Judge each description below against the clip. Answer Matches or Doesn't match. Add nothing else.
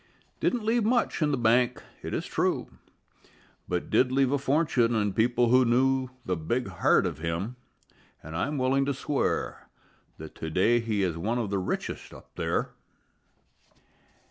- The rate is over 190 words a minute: Doesn't match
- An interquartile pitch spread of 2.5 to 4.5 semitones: Doesn't match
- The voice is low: Matches